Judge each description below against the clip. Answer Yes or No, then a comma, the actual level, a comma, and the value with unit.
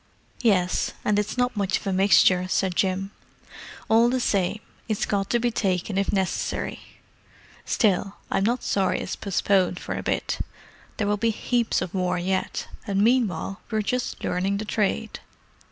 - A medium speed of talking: Yes, average, 165 wpm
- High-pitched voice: Yes, high, 200 Hz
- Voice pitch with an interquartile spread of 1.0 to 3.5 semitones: Yes, average, 2.8 semitones